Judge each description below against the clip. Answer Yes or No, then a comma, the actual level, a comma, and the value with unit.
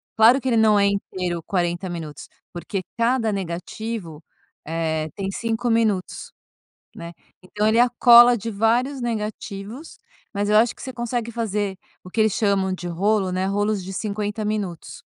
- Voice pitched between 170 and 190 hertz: No, high, 205 Hz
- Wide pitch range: No, average, 3.6 semitones